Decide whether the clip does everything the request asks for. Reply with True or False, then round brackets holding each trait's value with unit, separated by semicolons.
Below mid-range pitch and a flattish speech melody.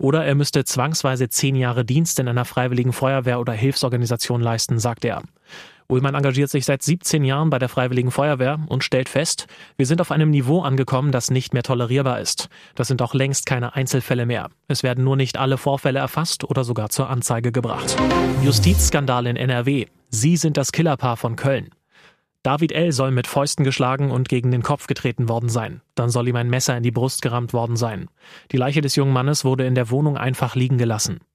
True (130 Hz; 2.2 semitones)